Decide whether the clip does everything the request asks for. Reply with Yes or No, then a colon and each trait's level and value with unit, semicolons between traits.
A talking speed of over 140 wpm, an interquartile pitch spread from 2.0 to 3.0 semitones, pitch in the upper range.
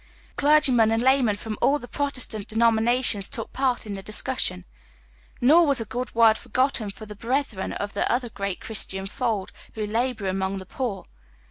No: average, 170 wpm; average, 3.9 semitones; high, 225 Hz